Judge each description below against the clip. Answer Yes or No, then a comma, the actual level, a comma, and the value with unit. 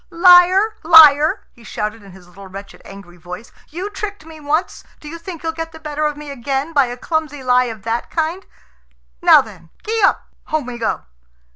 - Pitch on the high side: Yes, very high, 295 Hz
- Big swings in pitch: Yes, wide, 6.0 semitones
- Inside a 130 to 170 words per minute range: No, average, 195 wpm